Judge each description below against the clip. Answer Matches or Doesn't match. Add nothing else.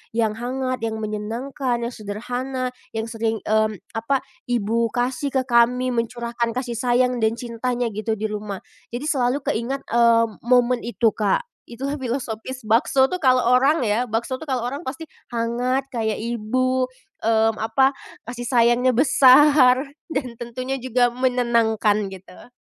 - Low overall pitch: Doesn't match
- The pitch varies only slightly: Matches